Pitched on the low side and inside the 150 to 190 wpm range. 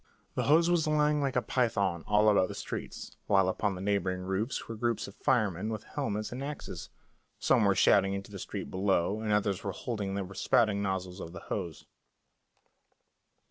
Yes: low, 100 Hz; average, 180 wpm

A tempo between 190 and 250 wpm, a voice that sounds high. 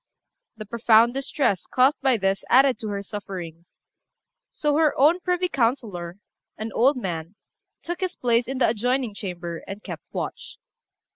No: average, 150 wpm; high, 235 Hz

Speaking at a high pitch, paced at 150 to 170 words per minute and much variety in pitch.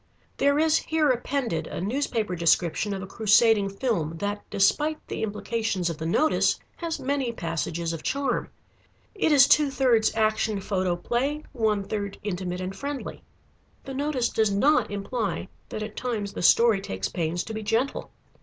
Yes: high, 220 Hz; average, 160 wpm; wide, 5.8 semitones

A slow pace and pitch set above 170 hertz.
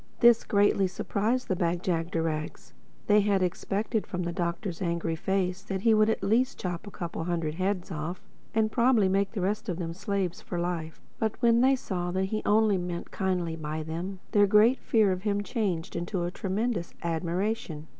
No: average, 185 wpm; high, 190 Hz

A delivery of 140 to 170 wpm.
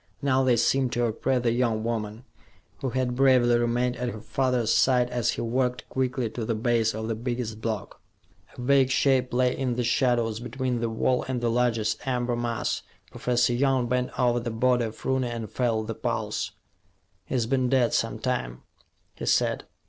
No: average, 185 wpm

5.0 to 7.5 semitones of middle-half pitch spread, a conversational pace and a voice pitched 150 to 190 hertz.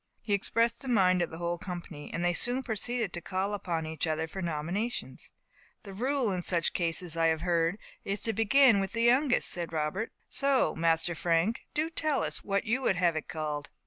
No: wide, 5.6 semitones; fast, 210 wpm; medium, 185 Hz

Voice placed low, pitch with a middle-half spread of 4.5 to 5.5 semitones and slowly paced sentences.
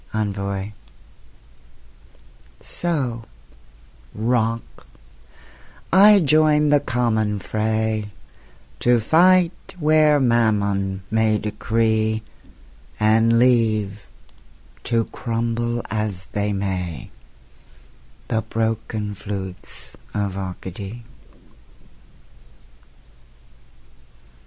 No: low, 110 Hz; average, 2.7 semitones; slow, 65 wpm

